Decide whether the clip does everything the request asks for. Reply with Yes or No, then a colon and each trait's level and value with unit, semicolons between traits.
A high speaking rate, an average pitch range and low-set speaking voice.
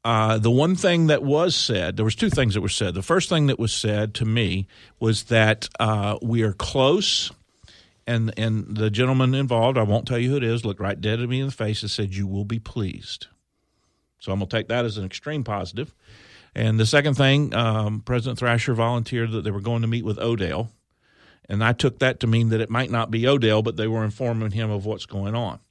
No: fast, 235 wpm; narrow, 2.3 semitones; low, 115 Hz